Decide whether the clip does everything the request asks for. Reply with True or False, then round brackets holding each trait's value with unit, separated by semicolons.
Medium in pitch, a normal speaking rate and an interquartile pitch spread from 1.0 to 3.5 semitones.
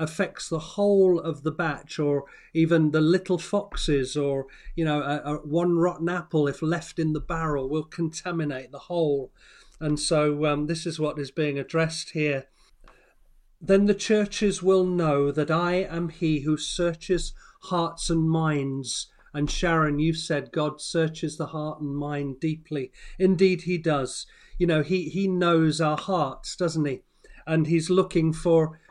True (160 Hz; 165 wpm; 2.6 semitones)